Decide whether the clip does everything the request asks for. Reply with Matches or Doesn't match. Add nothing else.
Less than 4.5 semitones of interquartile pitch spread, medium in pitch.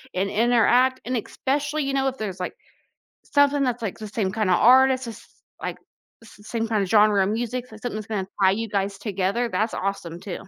Doesn't match